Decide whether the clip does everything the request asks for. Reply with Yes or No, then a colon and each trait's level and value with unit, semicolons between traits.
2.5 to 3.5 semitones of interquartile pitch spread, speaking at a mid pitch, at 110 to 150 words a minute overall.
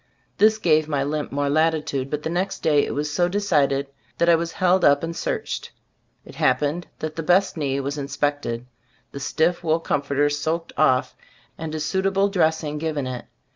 No: average, 2.9 semitones; medium, 155 Hz; average, 180 wpm